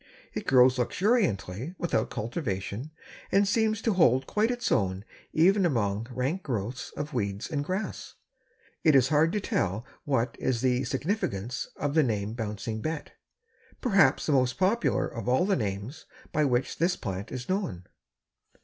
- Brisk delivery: No, average, 155 wpm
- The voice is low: Yes, low, 130 Hz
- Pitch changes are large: Yes, wide, 7.7 semitones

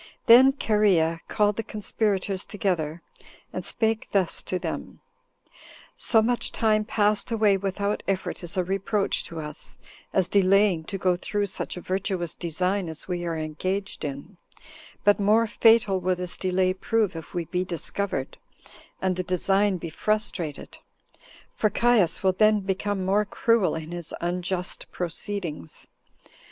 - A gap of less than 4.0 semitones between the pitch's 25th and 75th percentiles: Yes, average, 3.0 semitones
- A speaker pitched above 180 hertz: Yes, high, 190 Hz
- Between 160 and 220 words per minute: No, average, 145 wpm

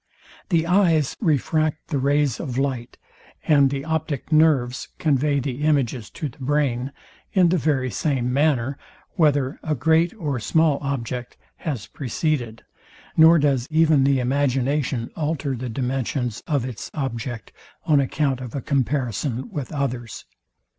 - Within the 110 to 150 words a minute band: Yes, average, 140 wpm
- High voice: No, medium, 140 Hz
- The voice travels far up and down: No, average, 3.3 semitones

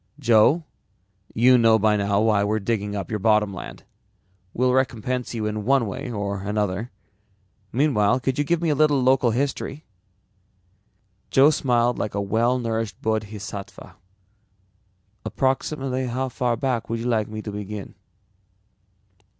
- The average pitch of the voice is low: Yes, low, 115 Hz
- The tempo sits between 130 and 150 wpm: Yes, average, 140 wpm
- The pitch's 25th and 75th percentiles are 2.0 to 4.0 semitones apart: Yes, average, 3.6 semitones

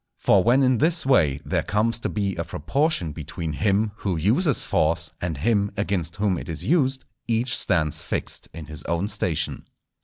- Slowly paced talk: No, average, 180 wpm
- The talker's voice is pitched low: Yes, low, 100 Hz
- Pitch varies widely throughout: Yes, wide, 6.2 semitones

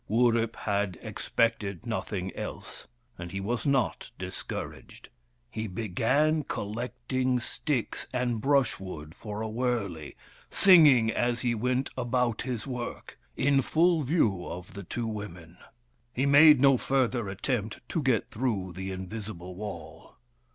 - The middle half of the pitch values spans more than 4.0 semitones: Yes, average, 4.4 semitones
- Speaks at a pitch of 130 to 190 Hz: No, low, 115 Hz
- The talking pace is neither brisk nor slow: No, slow, 130 wpm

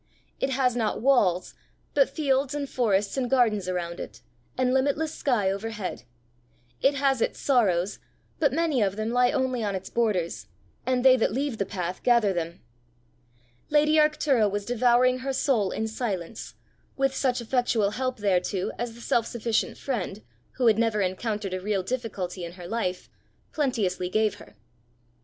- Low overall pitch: No, high, 230 Hz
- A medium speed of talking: Yes, average, 160 wpm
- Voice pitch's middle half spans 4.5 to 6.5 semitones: Yes, average, 4.9 semitones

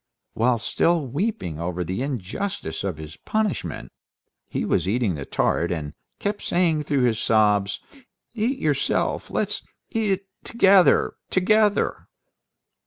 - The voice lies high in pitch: No, low, 135 Hz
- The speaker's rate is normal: No, slow, 125 wpm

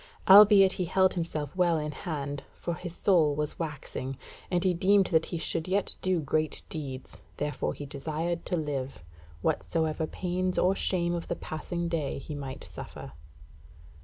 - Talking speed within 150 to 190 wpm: Yes, average, 160 wpm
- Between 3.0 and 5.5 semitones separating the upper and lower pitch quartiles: Yes, average, 3.5 semitones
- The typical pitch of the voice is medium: Yes, medium, 165 Hz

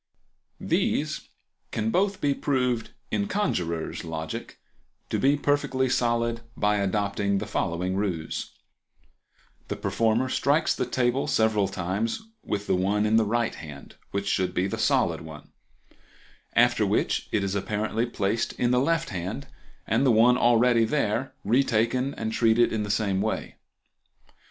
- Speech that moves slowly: No, average, 145 wpm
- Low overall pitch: Yes, low, 110 Hz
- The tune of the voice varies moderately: Yes, average, 3.9 semitones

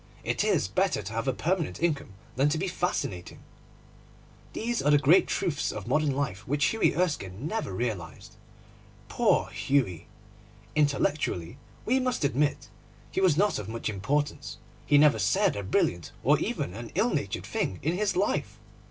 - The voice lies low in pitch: No, medium, 145 Hz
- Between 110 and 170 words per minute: Yes, average, 160 wpm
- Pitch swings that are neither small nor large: No, wide, 7.7 semitones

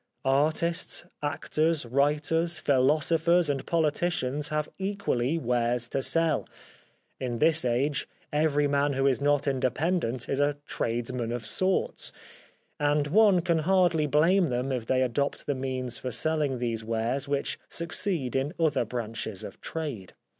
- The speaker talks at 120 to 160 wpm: Yes, average, 145 wpm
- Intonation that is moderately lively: Yes, average, 4.2 semitones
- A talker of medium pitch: Yes, medium, 145 Hz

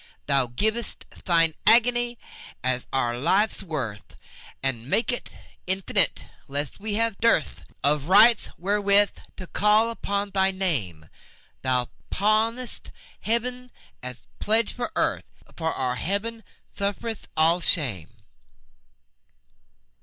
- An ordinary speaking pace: No, slow, 105 wpm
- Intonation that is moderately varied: No, wide, 8.1 semitones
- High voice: Yes, high, 195 Hz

